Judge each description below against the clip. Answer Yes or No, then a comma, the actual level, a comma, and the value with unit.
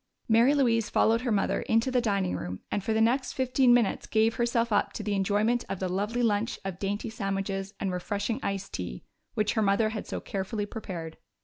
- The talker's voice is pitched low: No, high, 210 Hz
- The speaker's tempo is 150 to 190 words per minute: No, fast, 205 wpm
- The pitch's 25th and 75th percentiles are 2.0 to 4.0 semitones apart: Yes, average, 2.8 semitones